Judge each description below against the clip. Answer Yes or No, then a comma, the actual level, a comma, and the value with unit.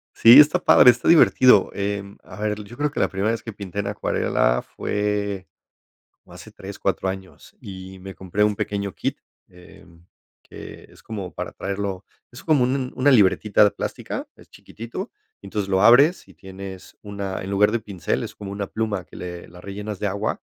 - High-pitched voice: No, low, 100 Hz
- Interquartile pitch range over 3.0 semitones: No, average, 2.7 semitones